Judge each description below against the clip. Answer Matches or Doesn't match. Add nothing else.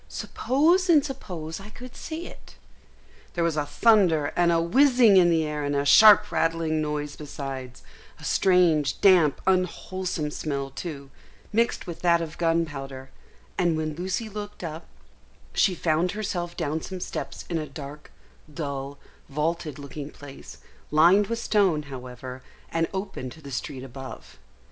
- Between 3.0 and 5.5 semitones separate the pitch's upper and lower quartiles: Matches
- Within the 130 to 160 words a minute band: Matches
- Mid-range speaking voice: Matches